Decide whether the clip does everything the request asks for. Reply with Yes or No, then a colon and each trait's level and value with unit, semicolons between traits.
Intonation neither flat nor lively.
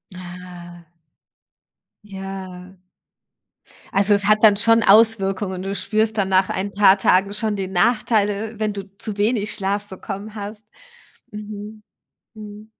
No: narrow, 1.8 semitones